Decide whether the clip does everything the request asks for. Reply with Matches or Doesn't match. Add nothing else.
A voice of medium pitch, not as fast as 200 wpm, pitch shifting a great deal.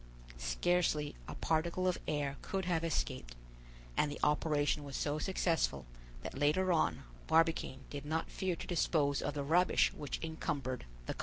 Doesn't match